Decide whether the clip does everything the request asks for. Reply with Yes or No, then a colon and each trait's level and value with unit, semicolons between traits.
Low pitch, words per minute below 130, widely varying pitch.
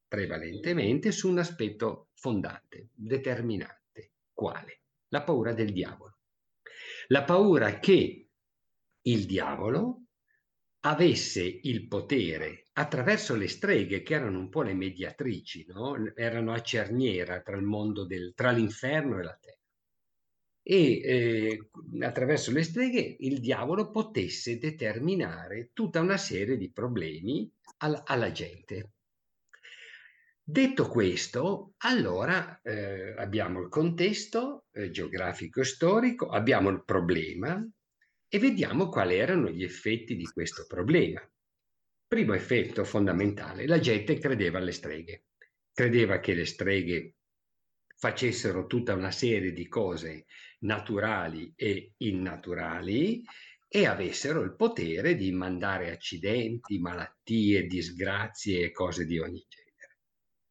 Yes: low, 110 Hz; slow, 115 wpm; wide, 7.8 semitones